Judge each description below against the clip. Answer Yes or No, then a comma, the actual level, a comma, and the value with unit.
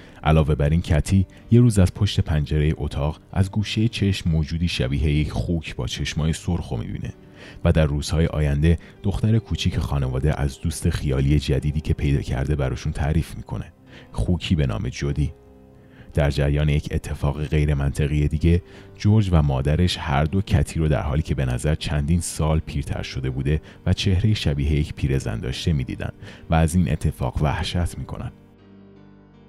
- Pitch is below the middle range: Yes, very low, 80 Hz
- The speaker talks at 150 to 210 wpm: Yes, fast, 155 wpm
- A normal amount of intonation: Yes, average, 4.6 semitones